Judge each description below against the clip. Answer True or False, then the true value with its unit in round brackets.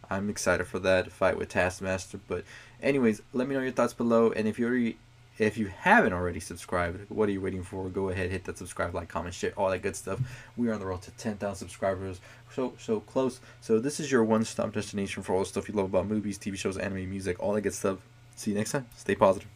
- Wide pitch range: False (3.6 semitones)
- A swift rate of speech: True (245 wpm)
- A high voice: False (105 Hz)